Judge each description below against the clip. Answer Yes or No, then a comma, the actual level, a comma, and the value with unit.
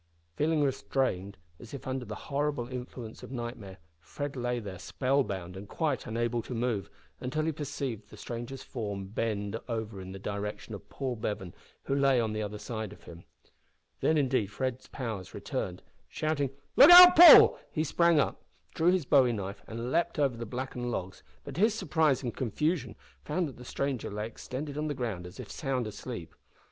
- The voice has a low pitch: Yes, low, 125 Hz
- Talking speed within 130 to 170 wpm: No, average, 185 wpm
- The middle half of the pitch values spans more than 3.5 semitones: Yes, average, 5.0 semitones